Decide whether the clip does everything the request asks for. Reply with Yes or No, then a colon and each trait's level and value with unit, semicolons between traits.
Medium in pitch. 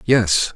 No: low, 105 Hz